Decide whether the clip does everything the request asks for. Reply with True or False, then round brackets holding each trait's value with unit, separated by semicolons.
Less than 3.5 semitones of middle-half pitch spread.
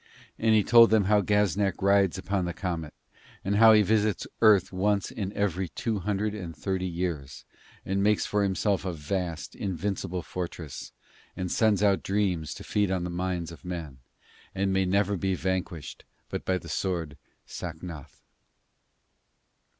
True (2.9 semitones)